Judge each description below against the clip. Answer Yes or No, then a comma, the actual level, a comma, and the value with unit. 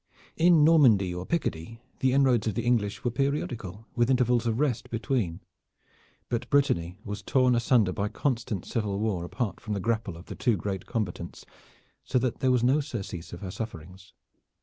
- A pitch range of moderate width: Yes, average, 4.7 semitones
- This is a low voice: Yes, low, 115 Hz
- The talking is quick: No, average, 175 wpm